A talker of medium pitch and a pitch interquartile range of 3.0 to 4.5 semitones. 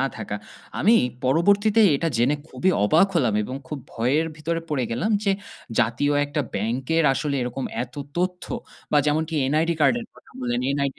No: medium, 150 Hz; average, 5.0 semitones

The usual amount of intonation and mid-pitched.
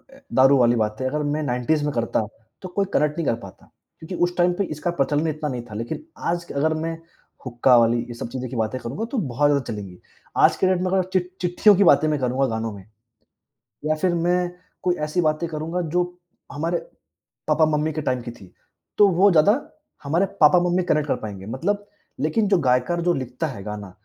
No: wide, 5.9 semitones; medium, 150 Hz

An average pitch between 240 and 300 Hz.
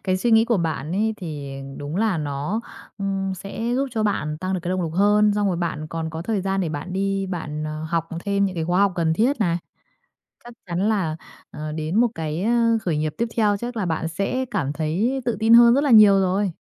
No: high, 190 Hz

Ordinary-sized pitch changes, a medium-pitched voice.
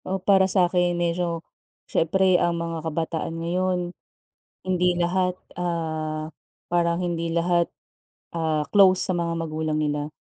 No: narrow, 1.7 semitones; medium, 170 Hz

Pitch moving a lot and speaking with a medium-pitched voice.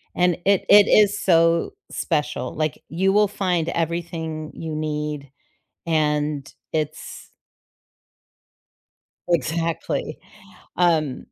No: narrow, 2.5 semitones; medium, 165 Hz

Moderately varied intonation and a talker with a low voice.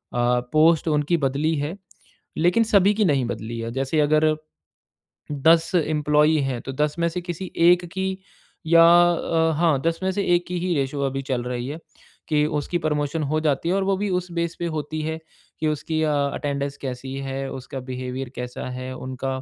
No: average, 3.9 semitones; medium, 150 Hz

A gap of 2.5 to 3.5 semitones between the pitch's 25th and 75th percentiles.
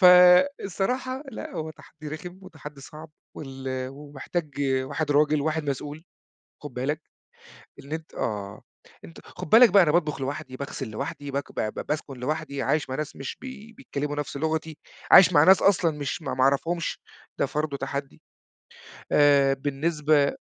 Yes: average, 3.2 semitones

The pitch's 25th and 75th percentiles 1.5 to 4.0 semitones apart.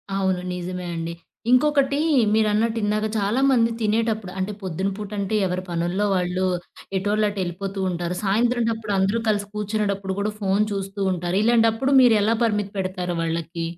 Yes: average, 3.0 semitones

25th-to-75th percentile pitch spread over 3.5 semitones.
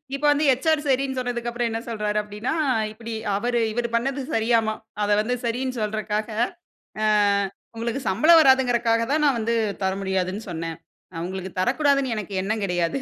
Yes: average, 3.9 semitones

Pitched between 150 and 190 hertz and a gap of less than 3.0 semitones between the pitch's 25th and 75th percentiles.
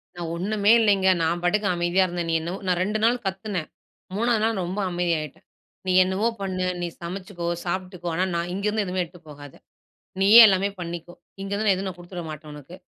Yes: medium, 185 Hz; narrow, 2.4 semitones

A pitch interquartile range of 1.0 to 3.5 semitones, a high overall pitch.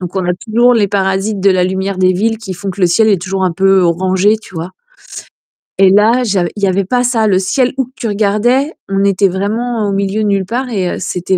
Yes: average, 2.7 semitones; high, 195 Hz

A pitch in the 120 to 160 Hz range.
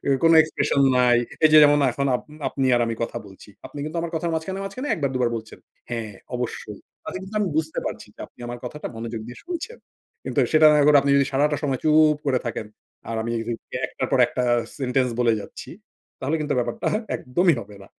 Yes: medium, 140 Hz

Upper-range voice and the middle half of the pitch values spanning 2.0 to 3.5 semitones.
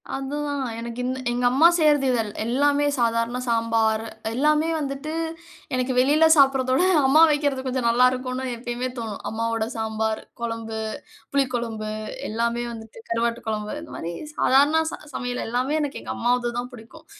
Yes: high, 245 Hz; average, 3.1 semitones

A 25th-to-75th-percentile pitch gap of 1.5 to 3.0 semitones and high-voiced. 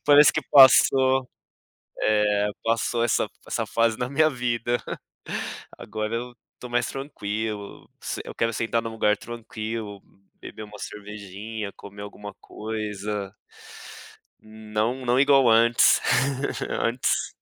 No: narrow, 2.6 semitones; low, 115 Hz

